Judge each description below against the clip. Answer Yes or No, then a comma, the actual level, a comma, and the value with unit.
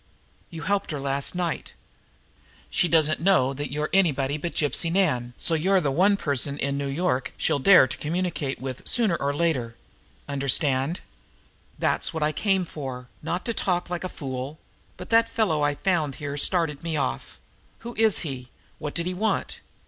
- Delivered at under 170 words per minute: No, average, 180 wpm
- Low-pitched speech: No, medium, 155 Hz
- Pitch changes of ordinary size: Yes, average, 4.6 semitones